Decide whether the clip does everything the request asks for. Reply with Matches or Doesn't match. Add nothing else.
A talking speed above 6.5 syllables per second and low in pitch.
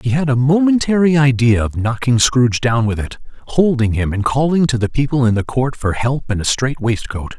Doesn't match